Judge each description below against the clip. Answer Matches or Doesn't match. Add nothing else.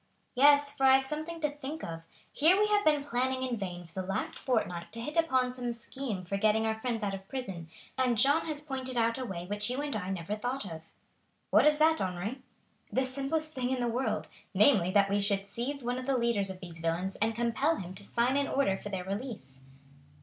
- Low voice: Doesn't match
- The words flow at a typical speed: Doesn't match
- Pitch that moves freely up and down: Matches